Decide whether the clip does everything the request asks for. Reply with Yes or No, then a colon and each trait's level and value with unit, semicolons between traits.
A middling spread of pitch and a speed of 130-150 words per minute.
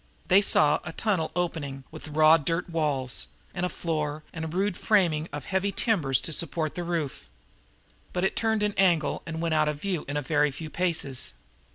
No: average, 3.2 semitones; average, 190 wpm